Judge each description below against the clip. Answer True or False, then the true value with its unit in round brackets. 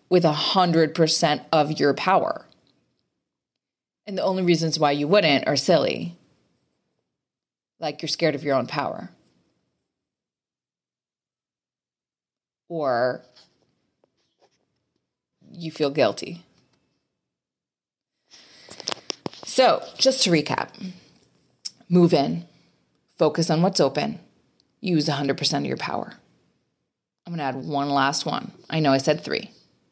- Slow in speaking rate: True (100 wpm)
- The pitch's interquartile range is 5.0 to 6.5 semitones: False (4.0 semitones)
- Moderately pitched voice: True (160 Hz)